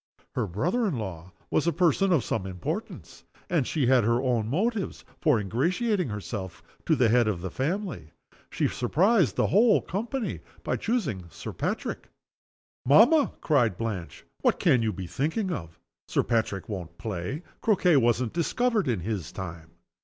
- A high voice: No, low, 125 Hz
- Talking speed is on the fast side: No, average, 160 wpm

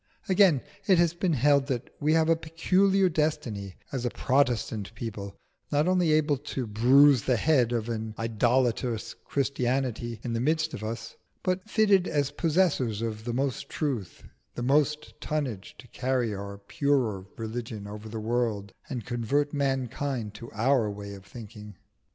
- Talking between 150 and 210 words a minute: Yes, average, 160 wpm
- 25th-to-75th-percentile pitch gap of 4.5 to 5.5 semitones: Yes, average, 5.0 semitones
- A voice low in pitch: Yes, low, 125 Hz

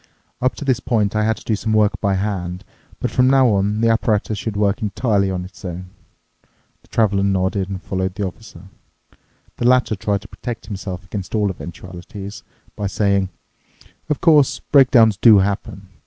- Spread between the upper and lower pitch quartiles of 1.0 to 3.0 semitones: Yes, average, 2.7 semitones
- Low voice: Yes, low, 100 Hz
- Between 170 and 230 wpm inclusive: Yes, average, 175 wpm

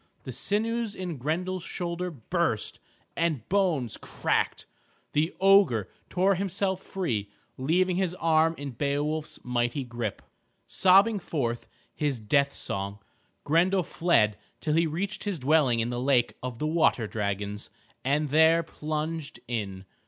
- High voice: No, medium, 155 Hz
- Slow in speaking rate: Yes, slow, 130 wpm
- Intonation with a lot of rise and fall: Yes, wide, 6.8 semitones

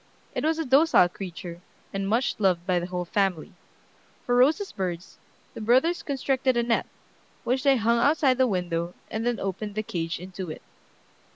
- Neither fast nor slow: Yes, average, 175 wpm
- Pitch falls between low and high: No, high, 215 Hz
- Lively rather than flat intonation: Yes, wide, 6.3 semitones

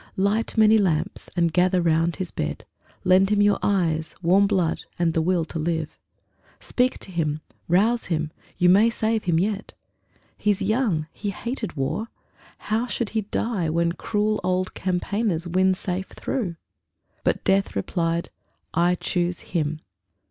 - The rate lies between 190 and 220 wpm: No, average, 150 wpm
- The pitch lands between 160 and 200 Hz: Yes, medium, 185 Hz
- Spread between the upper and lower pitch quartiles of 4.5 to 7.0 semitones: No, average, 3.7 semitones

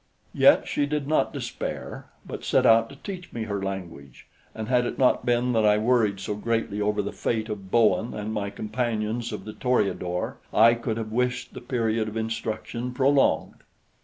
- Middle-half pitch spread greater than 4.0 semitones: No, average, 2.7 semitones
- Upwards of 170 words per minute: Yes, average, 185 wpm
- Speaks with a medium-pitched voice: No, low, 115 Hz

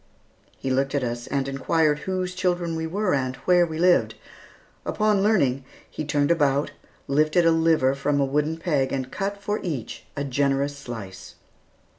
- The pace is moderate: Yes, average, 165 wpm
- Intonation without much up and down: No, average, 4.3 semitones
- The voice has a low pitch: No, medium, 150 Hz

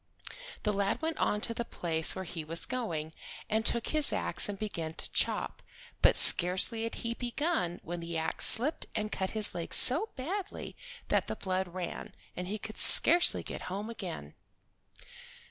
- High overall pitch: Yes, high, 205 Hz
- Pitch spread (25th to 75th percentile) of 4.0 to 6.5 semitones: Yes, average, 5.2 semitones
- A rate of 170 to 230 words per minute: Yes, average, 175 wpm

